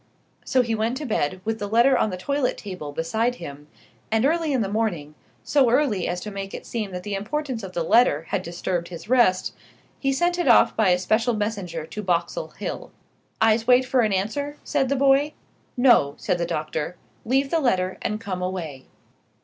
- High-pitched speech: Yes, high, 215 Hz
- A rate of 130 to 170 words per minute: No, average, 200 wpm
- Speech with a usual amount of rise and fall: No, wide, 6.0 semitones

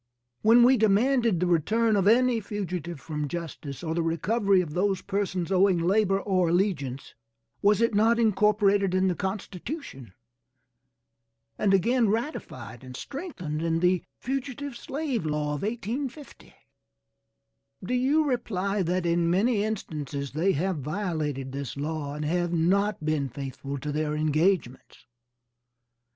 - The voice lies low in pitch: No, medium, 185 Hz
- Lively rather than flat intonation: Yes, wide, 5.8 semitones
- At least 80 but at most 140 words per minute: Yes, slow, 135 wpm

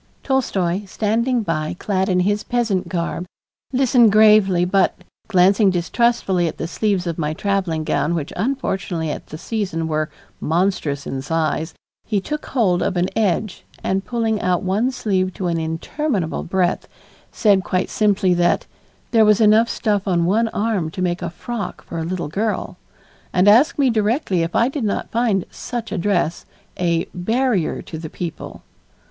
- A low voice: No, high, 190 Hz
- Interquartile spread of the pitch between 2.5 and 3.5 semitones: No, average, 4.2 semitones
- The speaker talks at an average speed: Yes, average, 165 wpm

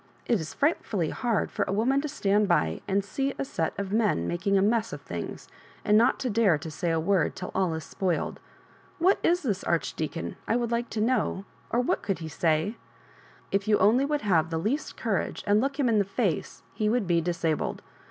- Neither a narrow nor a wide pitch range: No, wide, 5.8 semitones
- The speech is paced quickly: Yes, fast, 215 wpm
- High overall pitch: Yes, high, 200 Hz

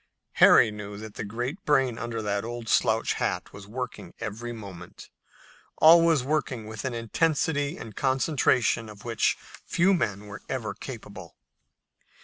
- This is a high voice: No, low, 115 Hz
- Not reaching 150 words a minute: Yes, average, 140 wpm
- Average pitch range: Yes, average, 4.4 semitones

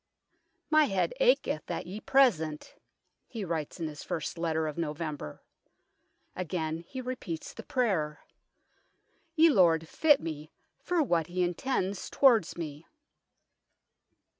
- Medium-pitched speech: Yes, medium, 175 Hz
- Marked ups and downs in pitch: Yes, wide, 8.1 semitones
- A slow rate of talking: Yes, slow, 130 wpm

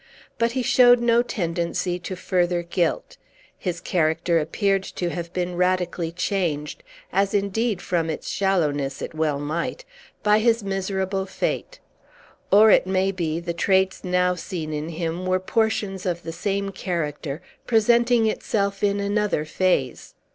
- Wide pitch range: No, average, 3.0 semitones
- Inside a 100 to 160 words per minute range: Yes, average, 145 wpm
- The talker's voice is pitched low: No, medium, 185 Hz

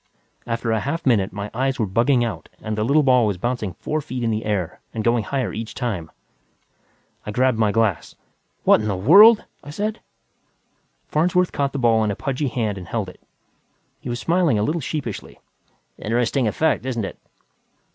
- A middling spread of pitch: Yes, average, 4.5 semitones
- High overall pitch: No, low, 120 Hz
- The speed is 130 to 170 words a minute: No, average, 185 wpm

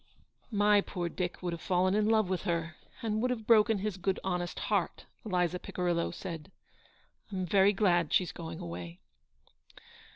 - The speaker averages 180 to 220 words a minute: No, average, 170 wpm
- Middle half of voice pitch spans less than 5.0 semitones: Yes, average, 3.2 semitones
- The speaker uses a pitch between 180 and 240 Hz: Yes, medium, 185 Hz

